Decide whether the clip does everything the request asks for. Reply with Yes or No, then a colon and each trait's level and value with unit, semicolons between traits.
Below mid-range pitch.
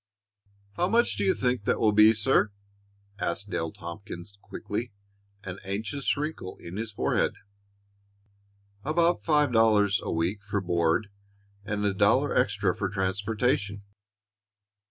Yes: low, 105 Hz